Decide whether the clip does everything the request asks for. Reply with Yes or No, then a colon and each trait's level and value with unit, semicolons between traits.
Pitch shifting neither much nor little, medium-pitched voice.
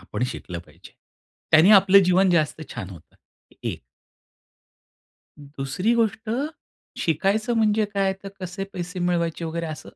Yes: average, 4.1 semitones; medium, 180 Hz